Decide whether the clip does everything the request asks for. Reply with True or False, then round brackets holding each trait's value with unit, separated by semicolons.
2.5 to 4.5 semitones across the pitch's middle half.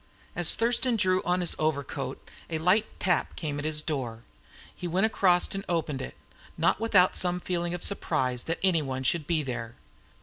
True (4.0 semitones)